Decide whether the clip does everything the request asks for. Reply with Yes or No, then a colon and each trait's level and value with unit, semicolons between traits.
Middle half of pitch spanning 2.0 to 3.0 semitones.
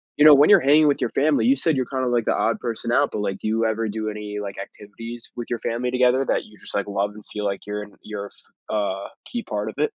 No: average, 3.6 semitones